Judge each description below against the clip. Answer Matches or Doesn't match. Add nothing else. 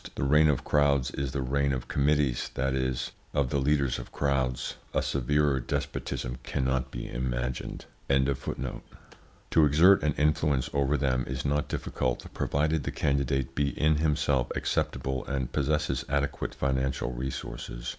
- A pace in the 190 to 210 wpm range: Doesn't match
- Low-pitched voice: Matches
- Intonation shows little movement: Matches